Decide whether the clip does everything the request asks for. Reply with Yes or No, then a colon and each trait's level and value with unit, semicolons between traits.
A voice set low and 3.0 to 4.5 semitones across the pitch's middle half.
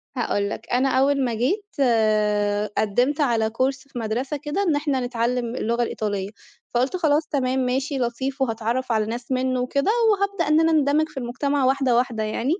No: very high, 255 Hz; average, 3.4 semitones